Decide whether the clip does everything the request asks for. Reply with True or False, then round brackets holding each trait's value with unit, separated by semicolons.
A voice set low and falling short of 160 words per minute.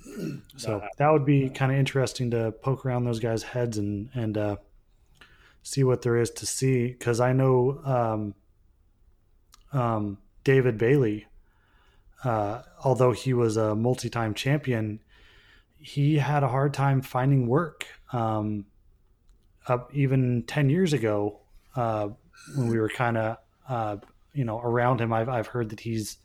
True (120 Hz; 150 wpm)